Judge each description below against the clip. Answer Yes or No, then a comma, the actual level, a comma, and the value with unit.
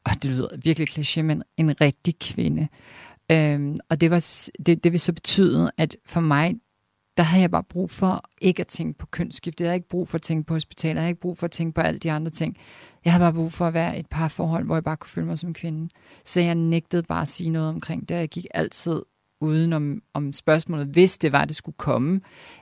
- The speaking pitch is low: No, medium, 165 Hz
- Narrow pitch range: Yes, narrow, 2.1 semitones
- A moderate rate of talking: No, fast, 250 wpm